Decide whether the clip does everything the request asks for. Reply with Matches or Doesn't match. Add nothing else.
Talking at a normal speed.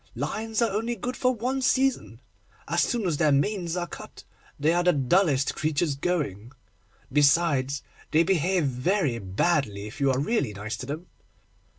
Matches